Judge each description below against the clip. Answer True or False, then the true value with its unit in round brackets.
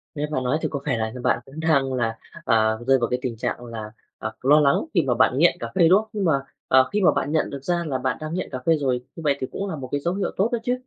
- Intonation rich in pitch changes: False (4.8 semitones)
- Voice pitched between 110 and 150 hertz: True (140 Hz)